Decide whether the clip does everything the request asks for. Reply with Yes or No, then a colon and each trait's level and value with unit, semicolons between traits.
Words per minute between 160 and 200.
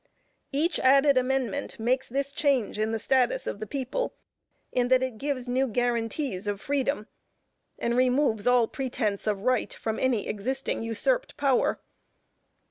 No: average, 145 wpm